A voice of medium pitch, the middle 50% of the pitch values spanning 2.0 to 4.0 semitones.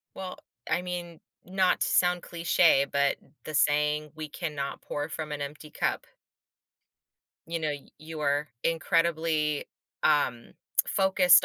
Yes: medium, 155 Hz; narrow, 2.6 semitones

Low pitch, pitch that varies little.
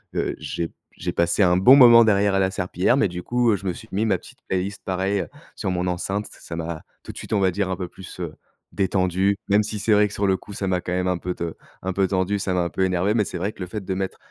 Yes: very low, 95 Hz; narrow, 2.1 semitones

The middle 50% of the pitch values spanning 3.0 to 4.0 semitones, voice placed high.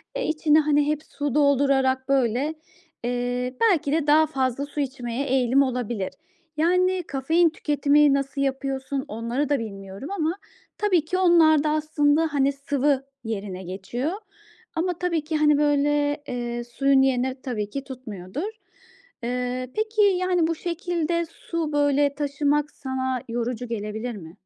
Yes: average, 3.6 semitones; very high, 280 Hz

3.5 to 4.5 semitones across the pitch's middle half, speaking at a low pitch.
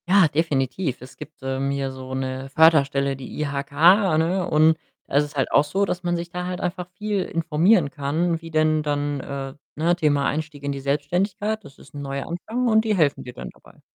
No: average, 4.1 semitones; medium, 150 Hz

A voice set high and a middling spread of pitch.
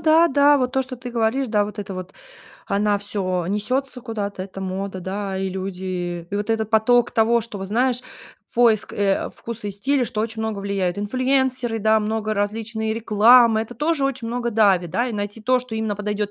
Yes: high, 220 Hz; average, 3.3 semitones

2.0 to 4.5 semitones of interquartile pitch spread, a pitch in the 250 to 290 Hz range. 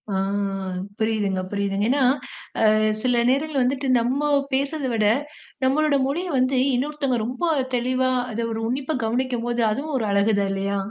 Yes: average, 3.9 semitones; very high, 255 Hz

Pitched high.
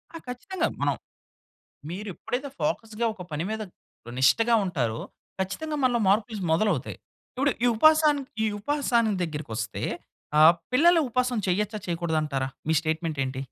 Yes: high, 210 Hz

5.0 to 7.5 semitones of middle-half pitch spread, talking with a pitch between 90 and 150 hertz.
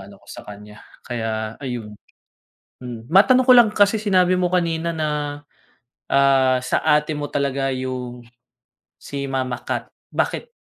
Yes: wide, 5.4 semitones; medium, 140 Hz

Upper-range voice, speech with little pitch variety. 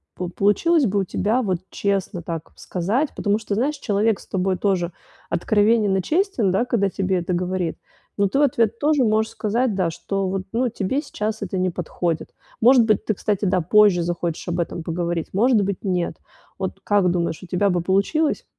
No: high, 195 Hz; average, 3.6 semitones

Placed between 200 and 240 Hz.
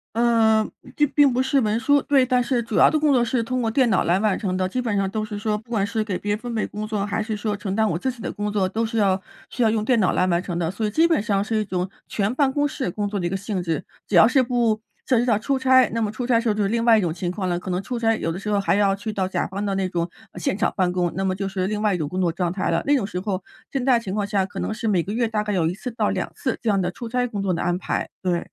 Yes: high, 210 Hz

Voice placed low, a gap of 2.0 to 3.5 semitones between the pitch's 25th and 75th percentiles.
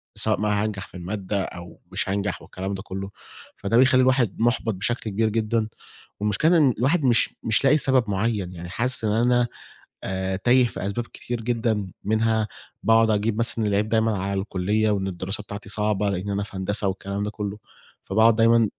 Yes: low, 105 Hz; average, 2.7 semitones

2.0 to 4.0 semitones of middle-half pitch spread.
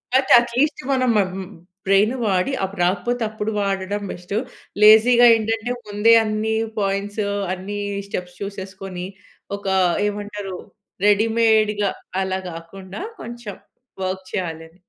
Yes: narrow, 2.6 semitones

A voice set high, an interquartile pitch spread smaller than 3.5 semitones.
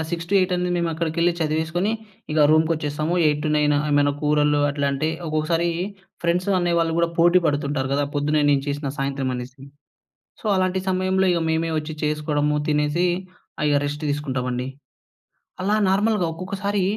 No: medium, 155 Hz; average, 2.9 semitones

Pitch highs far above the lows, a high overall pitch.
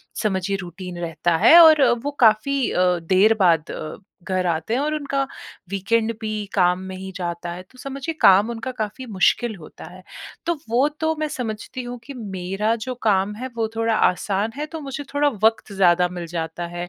Yes: wide, 5.7 semitones; high, 210 Hz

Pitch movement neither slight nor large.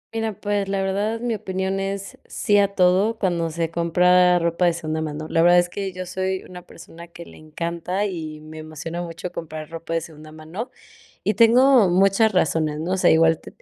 Yes: average, 3.1 semitones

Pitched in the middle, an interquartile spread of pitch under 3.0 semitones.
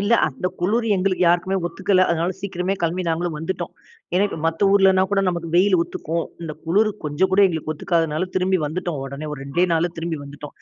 Yes: medium, 175 Hz; narrow, 2.6 semitones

